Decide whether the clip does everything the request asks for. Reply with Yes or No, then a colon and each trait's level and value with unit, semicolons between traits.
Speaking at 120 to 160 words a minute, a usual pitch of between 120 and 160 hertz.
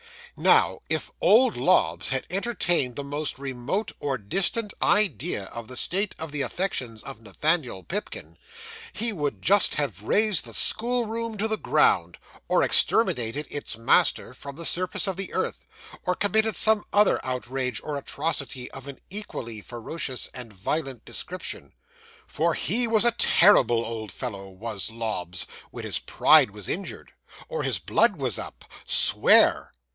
Yes: average, 150 wpm; medium, 140 Hz